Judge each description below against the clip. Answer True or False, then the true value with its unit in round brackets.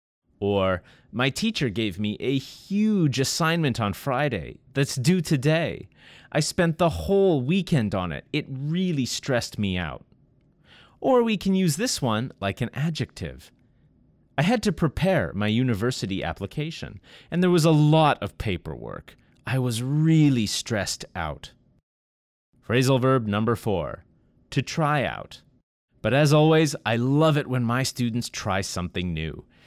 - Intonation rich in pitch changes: True (7.3 semitones)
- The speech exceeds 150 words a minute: False (145 wpm)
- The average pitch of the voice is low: True (130 Hz)